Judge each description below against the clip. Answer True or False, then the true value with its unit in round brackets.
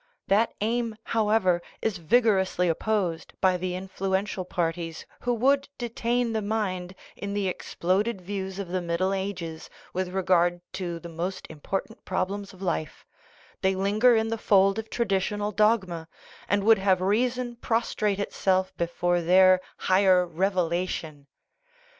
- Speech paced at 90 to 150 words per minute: True (140 wpm)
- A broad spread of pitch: False (2.9 semitones)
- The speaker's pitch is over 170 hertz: True (190 Hz)